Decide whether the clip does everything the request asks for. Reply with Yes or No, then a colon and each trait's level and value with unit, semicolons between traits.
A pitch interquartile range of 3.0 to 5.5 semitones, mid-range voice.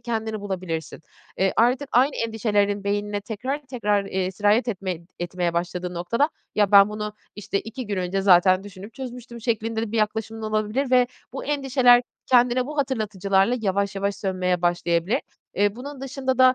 No: average, 4.1 semitones; high, 210 Hz